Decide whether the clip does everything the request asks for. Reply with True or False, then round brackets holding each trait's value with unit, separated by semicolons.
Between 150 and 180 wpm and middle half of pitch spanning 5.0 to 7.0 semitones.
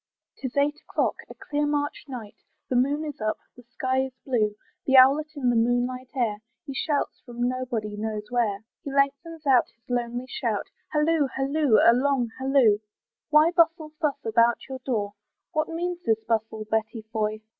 False (170 wpm; 4.2 semitones)